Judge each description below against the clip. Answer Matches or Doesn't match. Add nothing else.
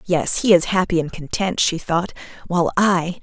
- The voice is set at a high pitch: Doesn't match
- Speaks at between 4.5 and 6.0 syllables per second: Matches